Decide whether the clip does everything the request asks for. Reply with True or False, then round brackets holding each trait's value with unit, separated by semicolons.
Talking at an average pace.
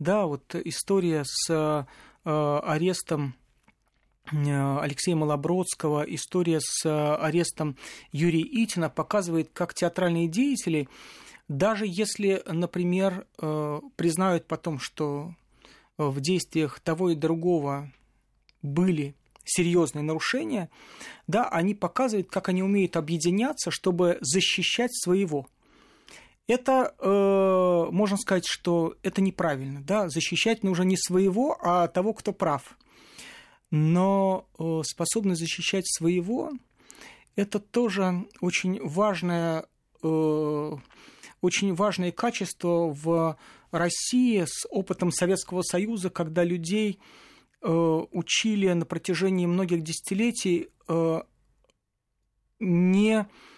False (95 wpm)